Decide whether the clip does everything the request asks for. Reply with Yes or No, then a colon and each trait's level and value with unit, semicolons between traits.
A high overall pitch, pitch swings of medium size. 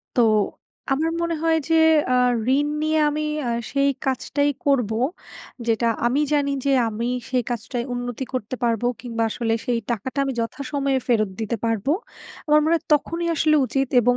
Yes: very high, 260 Hz; average, 3.7 semitones